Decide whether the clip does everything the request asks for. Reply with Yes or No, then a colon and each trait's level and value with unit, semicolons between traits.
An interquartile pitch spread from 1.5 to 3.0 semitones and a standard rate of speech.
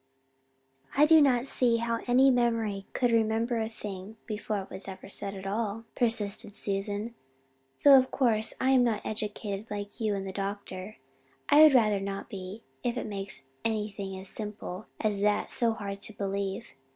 Yes: average, 2.7 semitones; average, 175 wpm